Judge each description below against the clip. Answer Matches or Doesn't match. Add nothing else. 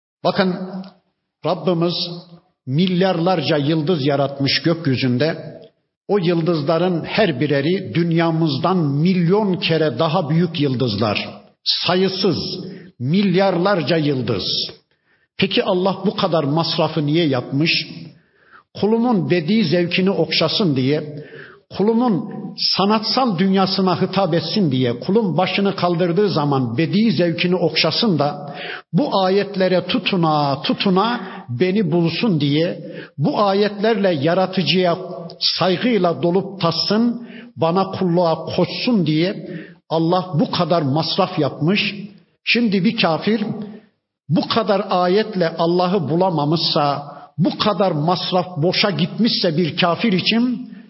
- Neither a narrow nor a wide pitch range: Matches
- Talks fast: Doesn't match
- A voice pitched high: Doesn't match